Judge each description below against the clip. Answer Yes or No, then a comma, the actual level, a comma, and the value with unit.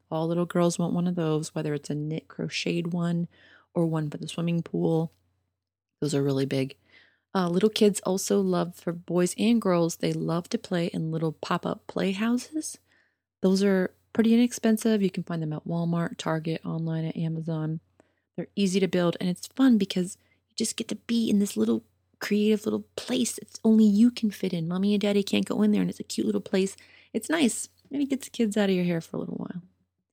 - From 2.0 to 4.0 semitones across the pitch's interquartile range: No, average, 4.6 semitones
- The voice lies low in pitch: No, medium, 180 Hz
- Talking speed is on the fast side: Yes, fast, 210 wpm